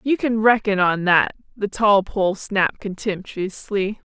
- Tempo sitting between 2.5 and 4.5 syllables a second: Yes, 4.1 syllables/s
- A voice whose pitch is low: No, high, 205 Hz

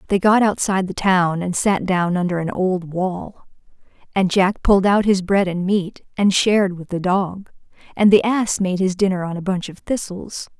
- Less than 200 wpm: No, fast, 205 wpm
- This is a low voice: No, high, 190 Hz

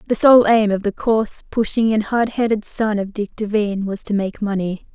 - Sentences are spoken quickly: Yes, fast, 220 wpm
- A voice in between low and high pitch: No, high, 210 Hz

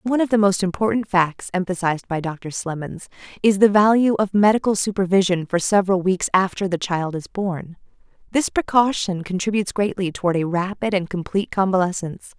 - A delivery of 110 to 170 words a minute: Yes, average, 165 wpm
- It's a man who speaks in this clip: No, female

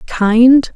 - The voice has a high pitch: Yes, high, 240 Hz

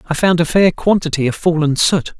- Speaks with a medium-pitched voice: Yes, medium, 165 Hz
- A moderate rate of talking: No, fast, 220 wpm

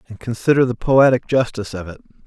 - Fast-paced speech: No, average, 185 wpm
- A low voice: Yes, low, 115 Hz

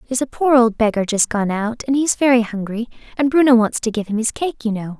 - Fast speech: Yes, fast, 240 wpm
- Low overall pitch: No, high, 235 Hz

